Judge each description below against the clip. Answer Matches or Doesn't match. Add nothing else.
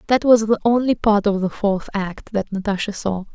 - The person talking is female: Matches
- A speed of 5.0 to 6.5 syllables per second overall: Matches